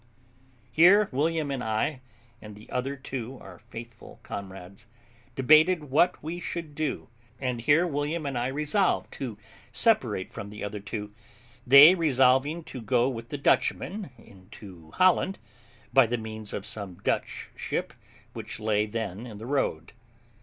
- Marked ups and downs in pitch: Yes, wide, 5.9 semitones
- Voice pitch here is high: No, low, 125 Hz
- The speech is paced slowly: No, average, 145 wpm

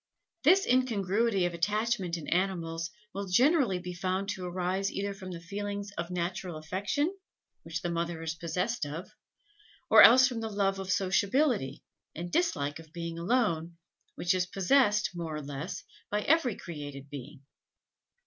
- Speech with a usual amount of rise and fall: Yes, average, 3.7 semitones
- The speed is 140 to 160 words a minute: Yes, average, 155 wpm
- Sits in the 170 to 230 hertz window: Yes, medium, 185 Hz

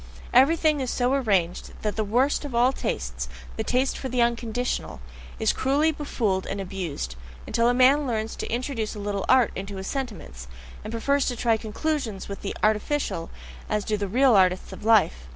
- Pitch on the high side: Yes, high, 225 Hz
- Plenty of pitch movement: No, average, 4.6 semitones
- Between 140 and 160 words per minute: No, average, 185 wpm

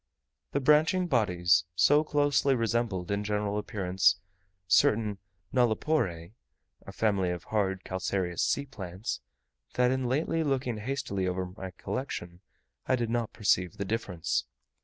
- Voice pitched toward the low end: Yes, low, 105 Hz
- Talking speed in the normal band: No, slow, 130 wpm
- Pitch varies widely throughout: Yes, wide, 5.7 semitones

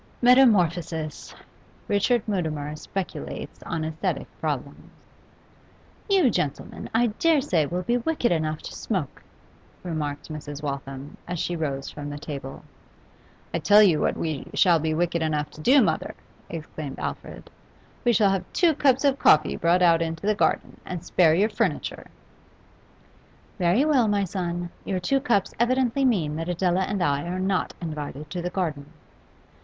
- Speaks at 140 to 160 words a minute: Yes, average, 155 wpm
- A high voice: No, medium, 175 Hz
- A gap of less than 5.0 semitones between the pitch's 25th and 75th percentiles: No, average, 5.3 semitones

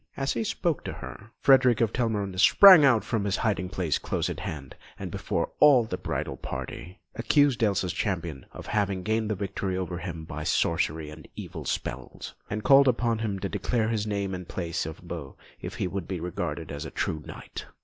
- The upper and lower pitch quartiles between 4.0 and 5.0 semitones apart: Yes, average, 4.7 semitones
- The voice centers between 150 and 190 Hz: No, low, 100 Hz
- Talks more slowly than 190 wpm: No, average, 200 wpm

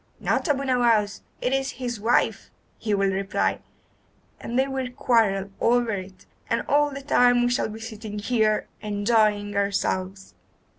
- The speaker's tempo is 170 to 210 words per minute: No, average, 150 wpm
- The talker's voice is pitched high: Yes, high, 225 Hz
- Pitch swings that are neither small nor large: Yes, average, 3.3 semitones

